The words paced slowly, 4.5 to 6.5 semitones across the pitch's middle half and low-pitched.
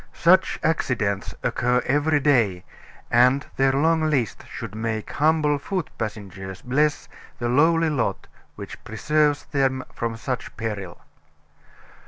Yes: slow, 120 wpm; average, 5.1 semitones; low, 130 Hz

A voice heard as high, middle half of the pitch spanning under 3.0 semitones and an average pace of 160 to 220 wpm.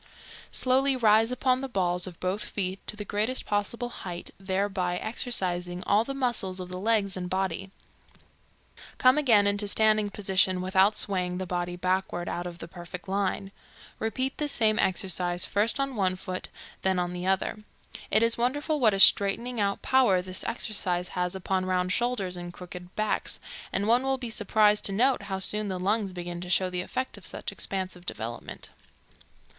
No: high, 195 Hz; average, 3.4 semitones; average, 175 wpm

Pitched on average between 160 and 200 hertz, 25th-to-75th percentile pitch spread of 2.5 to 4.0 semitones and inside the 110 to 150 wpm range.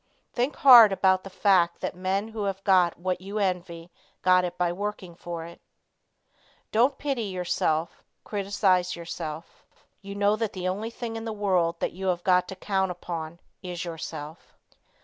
No: medium, 185 Hz; average, 2.8 semitones; average, 170 wpm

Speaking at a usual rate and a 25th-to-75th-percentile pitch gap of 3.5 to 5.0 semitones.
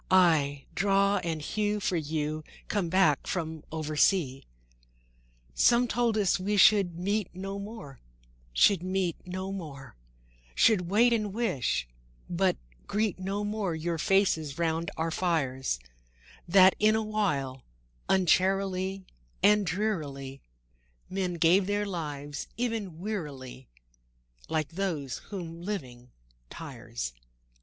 No: slow, 115 wpm; average, 4.5 semitones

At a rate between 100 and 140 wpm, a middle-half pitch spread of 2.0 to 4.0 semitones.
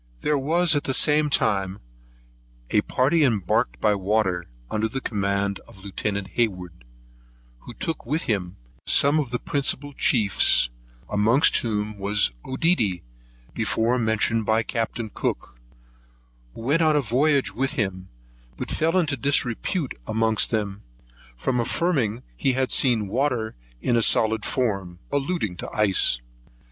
No: slow, 135 wpm; average, 5.3 semitones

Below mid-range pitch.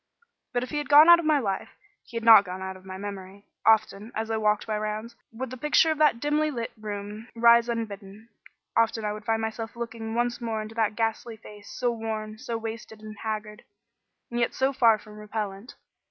No: high, 225 Hz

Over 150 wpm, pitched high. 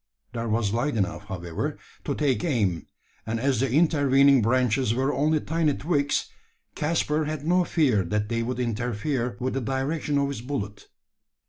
No: average, 160 wpm; low, 130 Hz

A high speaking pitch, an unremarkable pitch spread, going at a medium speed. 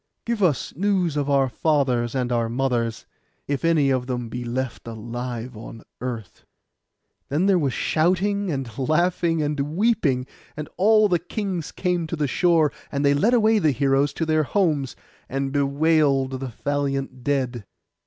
No: medium, 140 Hz; average, 4.7 semitones; average, 160 wpm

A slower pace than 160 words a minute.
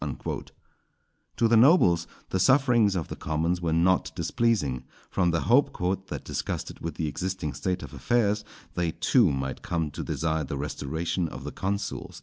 No: average, 165 wpm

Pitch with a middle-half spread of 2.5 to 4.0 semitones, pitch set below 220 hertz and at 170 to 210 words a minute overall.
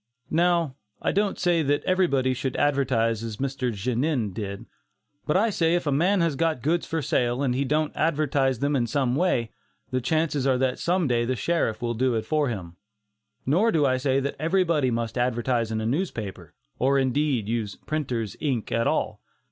No: average, 4.8 semitones; low, 135 Hz; average, 190 wpm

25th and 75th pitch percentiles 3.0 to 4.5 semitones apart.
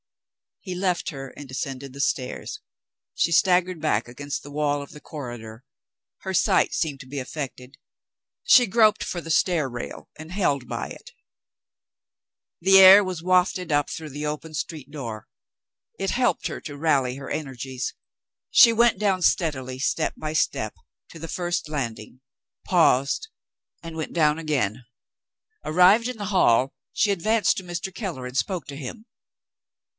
No: average, 5.3 semitones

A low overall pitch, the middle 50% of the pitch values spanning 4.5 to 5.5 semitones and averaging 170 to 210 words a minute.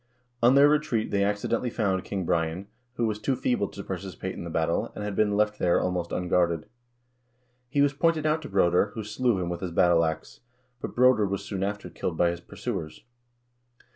Yes: low, 100 Hz; average, 5.1 semitones; average, 200 wpm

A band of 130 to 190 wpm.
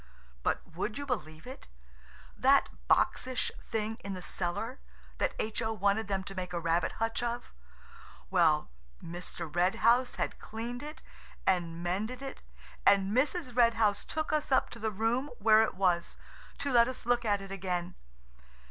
Yes: average, 155 wpm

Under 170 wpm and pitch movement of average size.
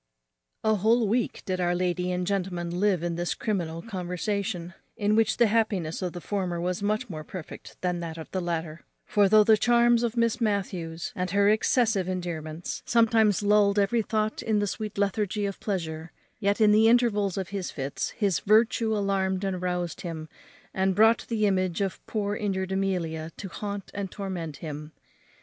No: average, 180 wpm; average, 3.3 semitones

